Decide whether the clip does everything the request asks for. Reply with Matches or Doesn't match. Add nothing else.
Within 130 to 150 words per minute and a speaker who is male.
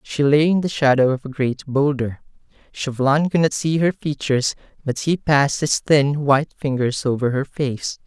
Doesn't match